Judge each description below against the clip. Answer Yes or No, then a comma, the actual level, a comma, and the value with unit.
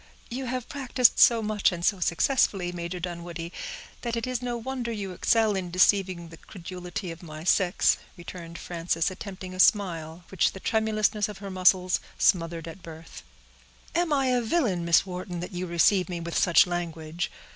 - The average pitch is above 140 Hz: Yes, medium, 185 Hz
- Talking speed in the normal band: Yes, average, 175 wpm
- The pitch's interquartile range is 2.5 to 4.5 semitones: Yes, average, 3.9 semitones